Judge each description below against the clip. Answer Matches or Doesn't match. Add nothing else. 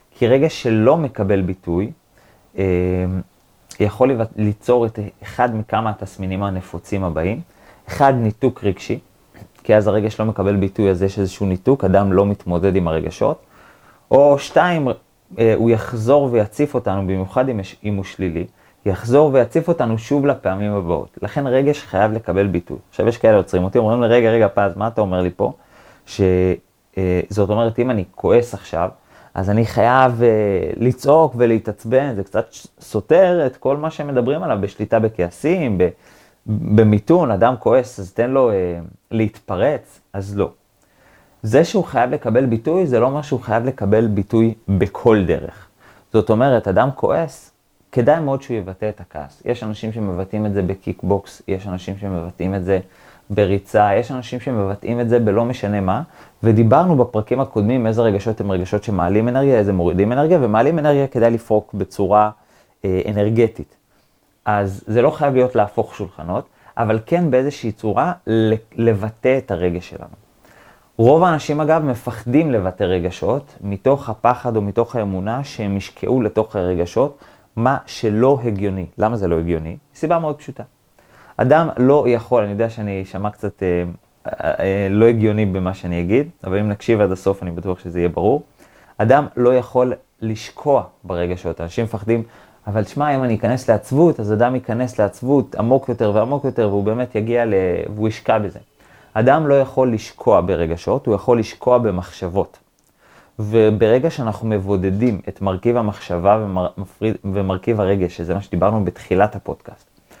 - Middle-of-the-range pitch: Doesn't match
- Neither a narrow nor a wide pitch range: Matches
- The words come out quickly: Matches